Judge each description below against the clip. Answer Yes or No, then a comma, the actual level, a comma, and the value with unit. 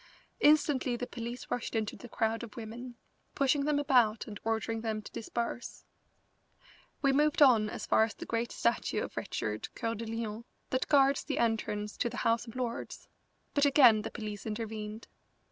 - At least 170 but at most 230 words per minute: Yes, average, 175 wpm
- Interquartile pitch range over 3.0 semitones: No, narrow, 2.6 semitones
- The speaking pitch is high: Yes, high, 230 Hz